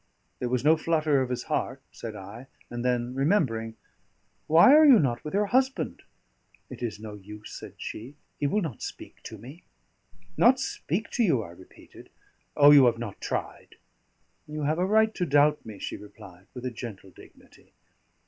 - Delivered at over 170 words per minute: Yes, average, 180 wpm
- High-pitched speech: No, low, 135 Hz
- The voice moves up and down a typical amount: No, wide, 6.6 semitones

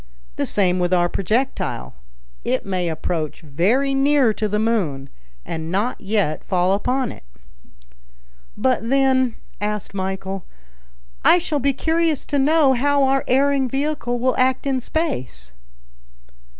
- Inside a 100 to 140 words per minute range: Yes, slow, 135 wpm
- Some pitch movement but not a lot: No, wide, 6.5 semitones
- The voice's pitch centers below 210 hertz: No, high, 235 Hz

